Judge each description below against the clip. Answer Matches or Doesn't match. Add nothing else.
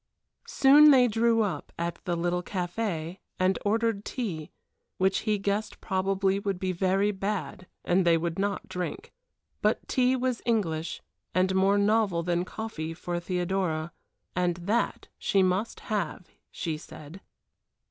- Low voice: Doesn't match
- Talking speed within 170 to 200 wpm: Doesn't match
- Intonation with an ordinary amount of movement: Matches